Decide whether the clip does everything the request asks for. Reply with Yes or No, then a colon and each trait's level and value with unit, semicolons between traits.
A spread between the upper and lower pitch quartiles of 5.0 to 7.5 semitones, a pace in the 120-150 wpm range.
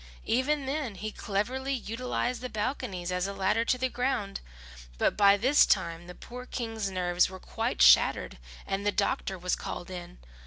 No: wide, 5.4 semitones; average, 170 wpm